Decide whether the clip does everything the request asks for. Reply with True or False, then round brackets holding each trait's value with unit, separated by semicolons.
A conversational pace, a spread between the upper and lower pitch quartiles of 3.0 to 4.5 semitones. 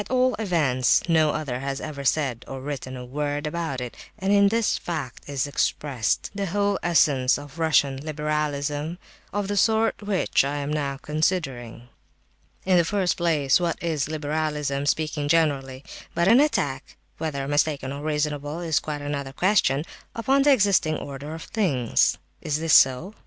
True (165 wpm; 3.8 semitones)